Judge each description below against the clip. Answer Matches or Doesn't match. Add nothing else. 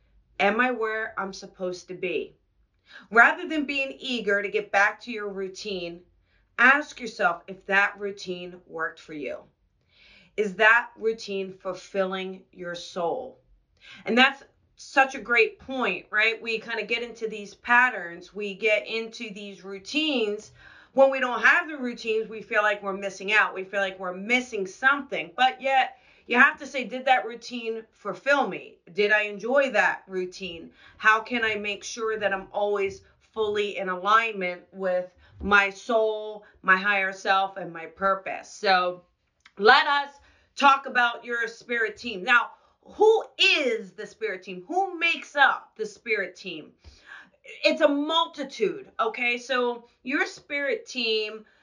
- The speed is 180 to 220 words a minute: Doesn't match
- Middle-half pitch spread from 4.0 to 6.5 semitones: Matches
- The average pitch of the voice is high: Matches